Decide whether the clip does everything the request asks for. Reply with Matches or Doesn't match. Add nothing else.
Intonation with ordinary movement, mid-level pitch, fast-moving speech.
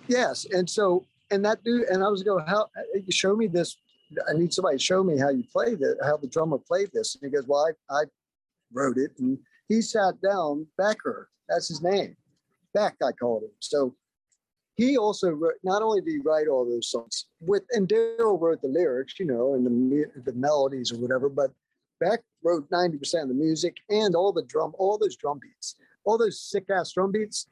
Doesn't match